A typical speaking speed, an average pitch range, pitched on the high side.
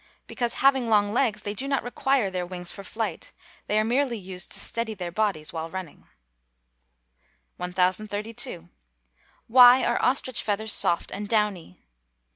Yes: average, 150 wpm; average, 4.4 semitones; high, 210 Hz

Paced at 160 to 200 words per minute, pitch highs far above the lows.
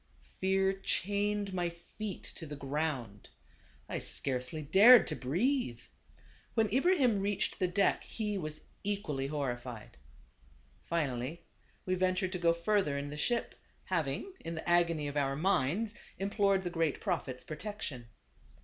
No: average, 150 wpm; wide, 5.7 semitones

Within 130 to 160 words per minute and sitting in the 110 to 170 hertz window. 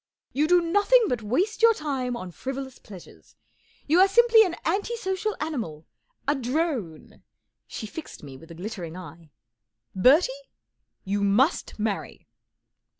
No: average, 150 wpm; very high, 270 Hz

